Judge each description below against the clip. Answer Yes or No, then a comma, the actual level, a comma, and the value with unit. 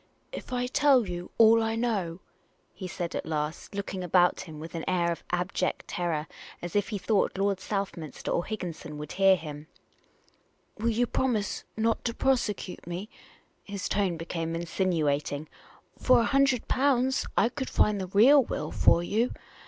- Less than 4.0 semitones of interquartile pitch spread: No, average, 5.0 semitones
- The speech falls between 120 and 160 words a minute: No, average, 175 wpm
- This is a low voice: No, high, 195 Hz